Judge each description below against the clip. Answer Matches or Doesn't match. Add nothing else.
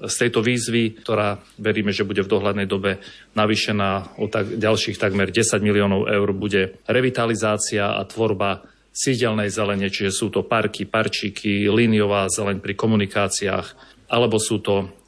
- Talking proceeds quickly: Doesn't match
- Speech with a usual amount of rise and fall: Doesn't match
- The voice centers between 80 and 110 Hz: Matches